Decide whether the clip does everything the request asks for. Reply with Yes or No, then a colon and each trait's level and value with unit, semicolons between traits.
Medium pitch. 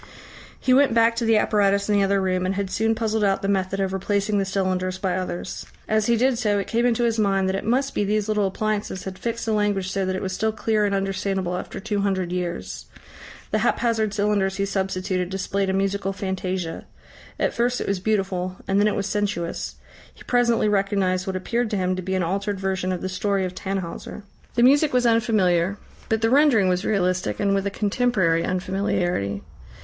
No: high, 195 Hz